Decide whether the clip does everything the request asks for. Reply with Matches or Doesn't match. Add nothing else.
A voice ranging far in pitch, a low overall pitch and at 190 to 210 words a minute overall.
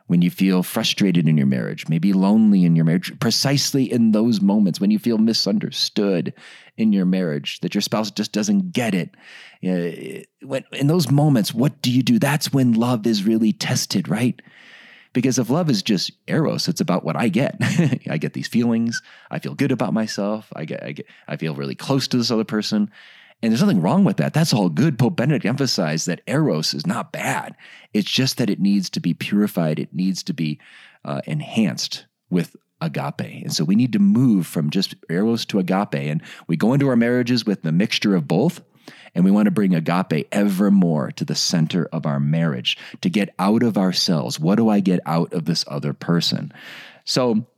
Matches